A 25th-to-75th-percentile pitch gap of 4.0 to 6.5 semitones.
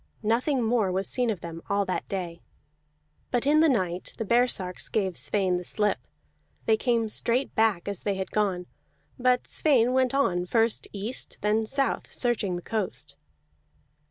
Yes: average, 4.6 semitones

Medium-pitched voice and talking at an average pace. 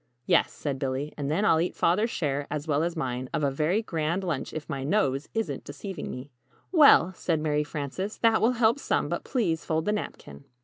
No: medium, 160 Hz; fast, 210 wpm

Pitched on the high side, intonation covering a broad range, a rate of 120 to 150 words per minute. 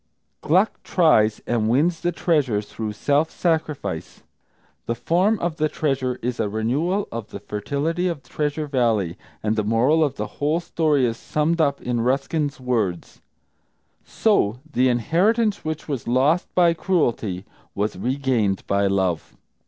No: low, 135 Hz; wide, 6.1 semitones; average, 145 wpm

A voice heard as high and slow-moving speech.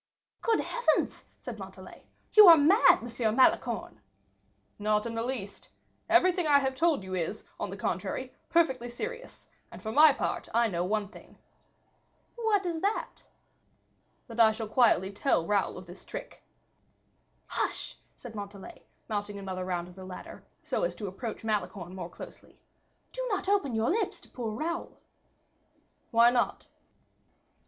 No: high, 230 Hz; average, 155 wpm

